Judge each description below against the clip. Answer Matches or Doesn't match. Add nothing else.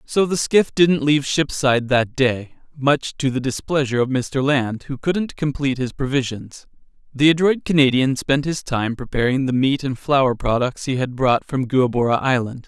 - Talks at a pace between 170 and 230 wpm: Matches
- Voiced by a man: Matches